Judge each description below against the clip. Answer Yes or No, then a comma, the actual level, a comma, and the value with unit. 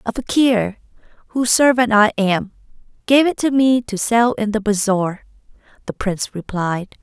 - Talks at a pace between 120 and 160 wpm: Yes, average, 155 wpm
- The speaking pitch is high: Yes, high, 220 Hz